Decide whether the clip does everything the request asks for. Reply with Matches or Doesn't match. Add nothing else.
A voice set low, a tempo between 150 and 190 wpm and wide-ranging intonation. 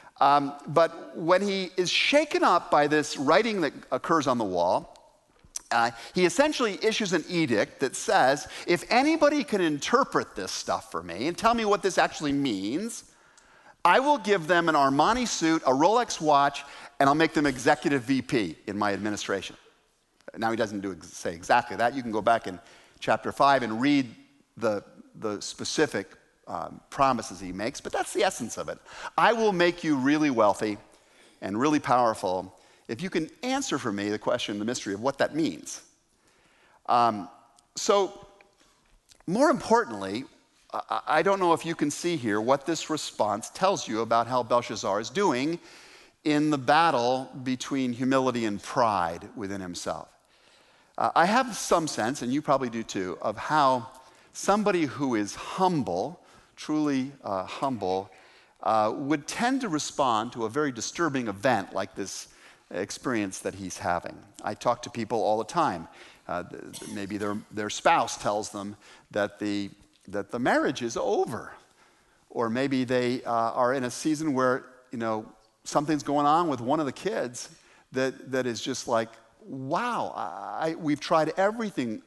Doesn't match